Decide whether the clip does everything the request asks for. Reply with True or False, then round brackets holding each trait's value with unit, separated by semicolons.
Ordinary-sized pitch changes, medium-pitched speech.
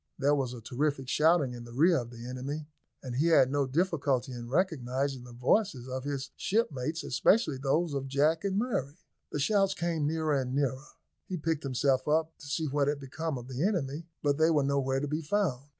True (3.6 semitones; 145 Hz)